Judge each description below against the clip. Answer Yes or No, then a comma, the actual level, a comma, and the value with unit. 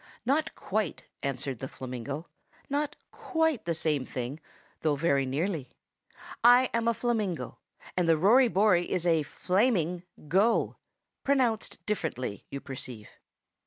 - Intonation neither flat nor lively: No, wide, 8.6 semitones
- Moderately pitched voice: Yes, medium, 175 Hz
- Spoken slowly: Yes, slow, 125 wpm